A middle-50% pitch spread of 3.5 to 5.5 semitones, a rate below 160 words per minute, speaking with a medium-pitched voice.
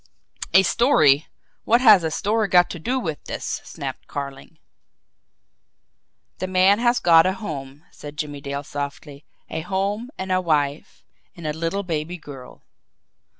Yes: average, 5.0 semitones; average, 150 wpm; medium, 165 Hz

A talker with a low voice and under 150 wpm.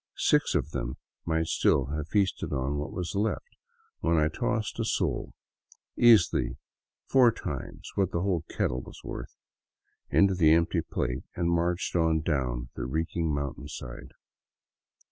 Yes: very low, 80 Hz; slow, 135 wpm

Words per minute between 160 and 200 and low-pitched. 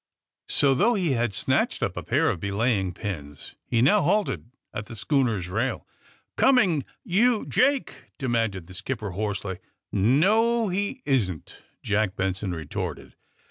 No: average, 145 wpm; low, 115 Hz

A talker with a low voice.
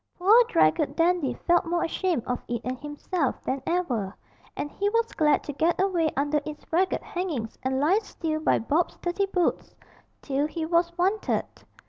No: very high, 325 Hz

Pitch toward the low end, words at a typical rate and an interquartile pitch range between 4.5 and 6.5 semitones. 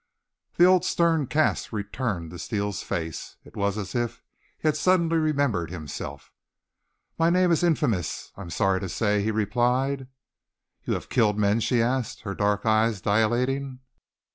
Yes: low, 115 Hz; average, 160 wpm; wide, 5.6 semitones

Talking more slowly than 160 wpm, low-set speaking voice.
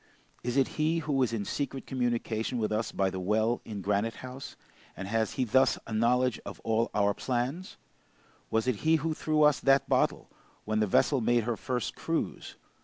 No: average, 190 wpm; low, 120 Hz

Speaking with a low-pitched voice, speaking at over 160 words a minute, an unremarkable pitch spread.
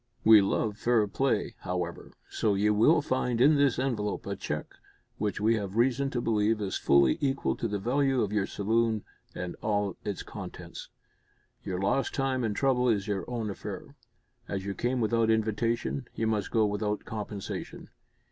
Yes: low, 110 Hz; average, 170 wpm; average, 3.1 semitones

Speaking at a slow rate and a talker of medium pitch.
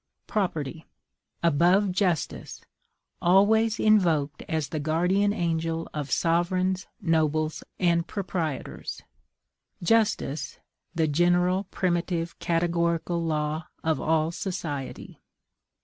Yes: slow, 85 wpm; medium, 170 Hz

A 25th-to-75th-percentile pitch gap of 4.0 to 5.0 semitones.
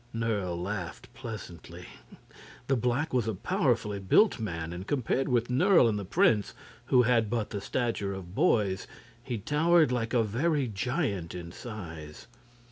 Yes: average, 4.5 semitones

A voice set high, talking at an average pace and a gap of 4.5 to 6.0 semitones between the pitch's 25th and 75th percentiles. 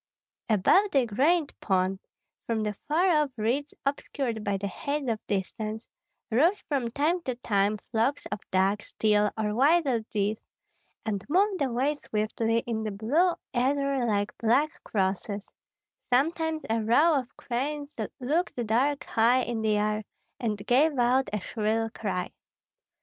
Yes: high, 235 Hz; average, 145 wpm; average, 5.2 semitones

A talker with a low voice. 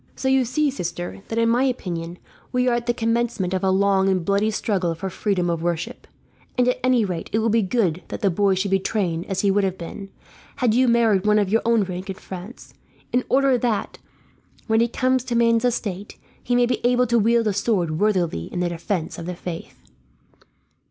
No: high, 205 Hz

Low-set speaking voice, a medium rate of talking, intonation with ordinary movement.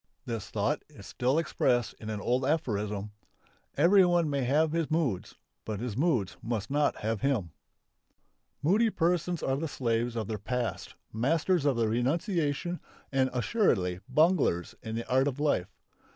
No: low, 130 Hz; average, 150 wpm; wide, 6.1 semitones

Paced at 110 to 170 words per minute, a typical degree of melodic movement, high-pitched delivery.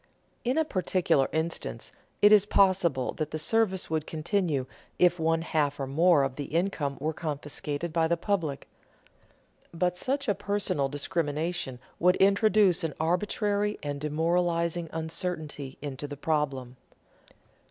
No: slow, 135 wpm; average, 4.0 semitones; medium, 165 Hz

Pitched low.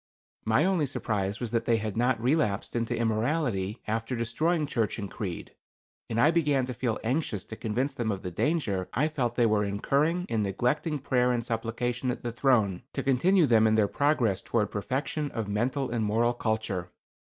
Yes: low, 120 Hz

